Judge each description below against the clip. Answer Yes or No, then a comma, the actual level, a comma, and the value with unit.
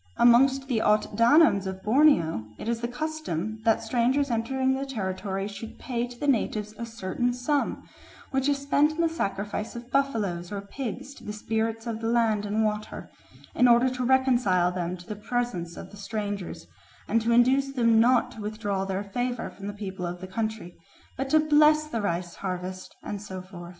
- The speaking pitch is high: Yes, high, 225 Hz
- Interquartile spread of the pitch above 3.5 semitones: Yes, average, 4.5 semitones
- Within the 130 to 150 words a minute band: No, average, 190 wpm